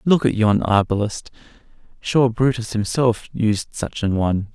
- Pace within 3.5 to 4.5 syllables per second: Yes, 4.4 syllables/s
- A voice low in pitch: Yes, low, 110 Hz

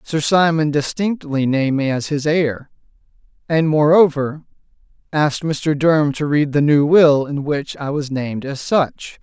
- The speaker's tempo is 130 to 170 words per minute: Yes, average, 165 wpm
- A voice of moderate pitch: Yes, medium, 150 Hz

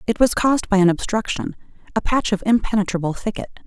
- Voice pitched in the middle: No, high, 210 Hz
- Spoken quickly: No, average, 165 wpm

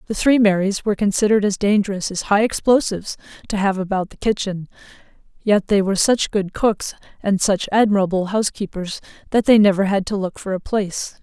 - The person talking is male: No, female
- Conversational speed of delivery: Yes, average, 180 wpm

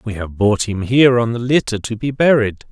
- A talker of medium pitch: No, low, 115 Hz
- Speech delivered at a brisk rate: Yes, fast, 245 wpm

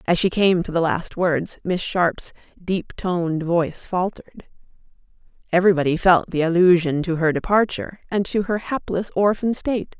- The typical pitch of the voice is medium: Yes, medium, 180 Hz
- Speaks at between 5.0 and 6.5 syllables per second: Yes, 5.1 syllables/s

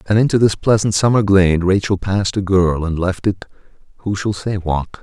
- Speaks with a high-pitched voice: No, very low, 95 Hz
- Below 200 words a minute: No, fast, 205 wpm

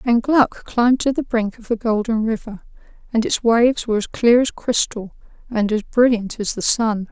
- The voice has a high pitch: Yes, high, 230 Hz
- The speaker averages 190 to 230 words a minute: Yes, average, 200 wpm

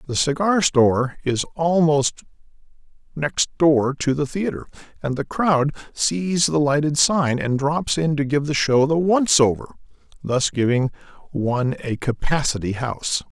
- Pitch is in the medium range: Yes, medium, 145 Hz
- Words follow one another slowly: No, average, 150 wpm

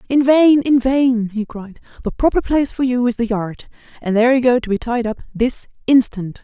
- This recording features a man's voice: No, female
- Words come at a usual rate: No, fast, 225 wpm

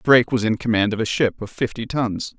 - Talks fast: Yes, fast, 250 wpm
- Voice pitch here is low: Yes, low, 115 Hz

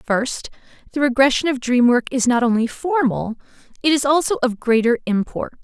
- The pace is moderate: Yes, average, 170 wpm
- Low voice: No, very high, 260 Hz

